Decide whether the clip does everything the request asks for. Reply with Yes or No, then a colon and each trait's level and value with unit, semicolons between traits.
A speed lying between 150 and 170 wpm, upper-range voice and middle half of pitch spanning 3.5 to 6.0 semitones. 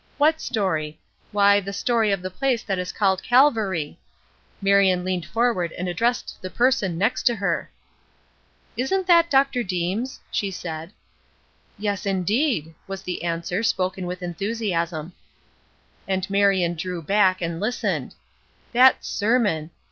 No: slow, 135 wpm; high, 195 Hz; average, 4.4 semitones